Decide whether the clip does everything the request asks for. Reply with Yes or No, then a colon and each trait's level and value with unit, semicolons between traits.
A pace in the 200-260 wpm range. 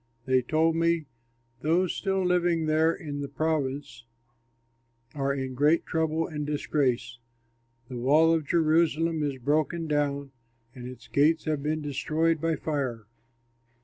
No: slow, 135 wpm